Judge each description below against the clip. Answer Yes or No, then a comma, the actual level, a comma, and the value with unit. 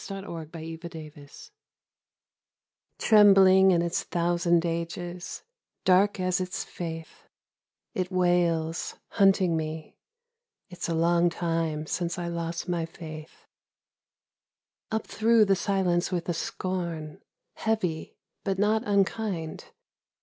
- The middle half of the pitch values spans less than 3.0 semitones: Yes, narrow, 2.5 semitones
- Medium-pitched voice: Yes, medium, 175 Hz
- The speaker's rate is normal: No, slow, 110 wpm